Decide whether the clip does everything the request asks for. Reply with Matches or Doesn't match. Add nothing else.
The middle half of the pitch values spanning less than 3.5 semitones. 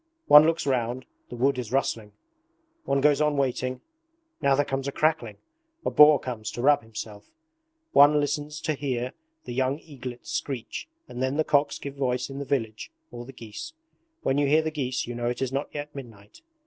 Matches